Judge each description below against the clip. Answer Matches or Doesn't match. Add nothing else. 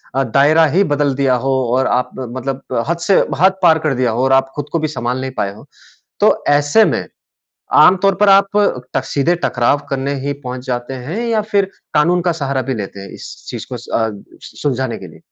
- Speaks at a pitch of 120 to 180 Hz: Matches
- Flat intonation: Doesn't match